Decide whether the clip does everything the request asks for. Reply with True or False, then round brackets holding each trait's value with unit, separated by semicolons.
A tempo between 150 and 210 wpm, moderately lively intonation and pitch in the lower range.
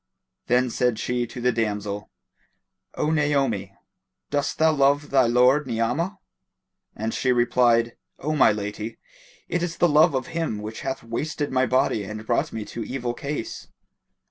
True (155 wpm; 4.2 semitones; 125 Hz)